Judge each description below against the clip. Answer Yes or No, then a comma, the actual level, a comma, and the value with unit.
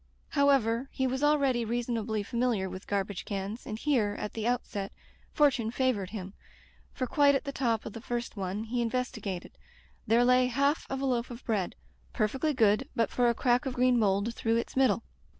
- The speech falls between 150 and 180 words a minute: No, average, 190 wpm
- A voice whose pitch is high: Yes, high, 235 Hz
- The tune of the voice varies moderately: Yes, average, 3.3 semitones